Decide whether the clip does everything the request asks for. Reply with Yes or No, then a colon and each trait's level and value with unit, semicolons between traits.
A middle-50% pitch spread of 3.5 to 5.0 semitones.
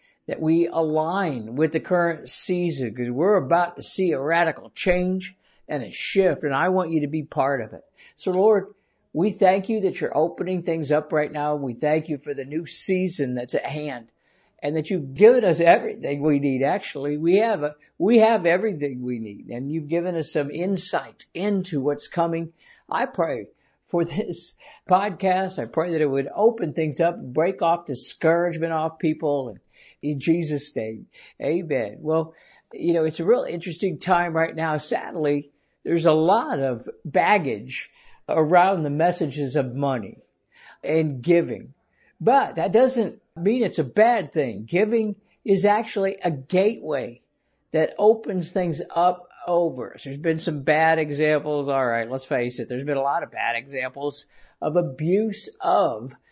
Yes: average, 4.0 semitones